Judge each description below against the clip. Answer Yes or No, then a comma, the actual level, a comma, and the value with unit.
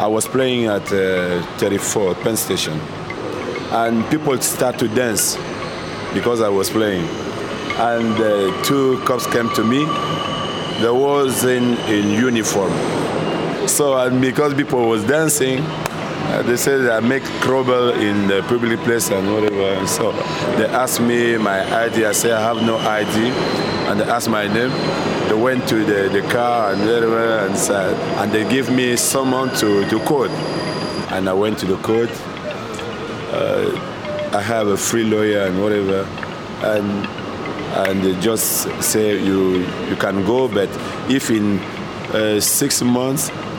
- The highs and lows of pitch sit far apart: No, average, 3.7 semitones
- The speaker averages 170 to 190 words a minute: No, average, 155 wpm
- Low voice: Yes, low, 115 Hz